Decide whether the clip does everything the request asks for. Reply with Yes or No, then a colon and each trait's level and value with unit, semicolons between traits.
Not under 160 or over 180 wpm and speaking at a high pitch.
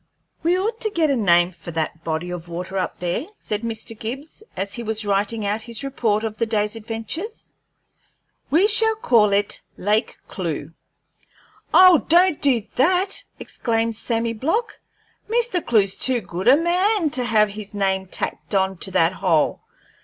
Yes: average, 165 wpm; high, 225 Hz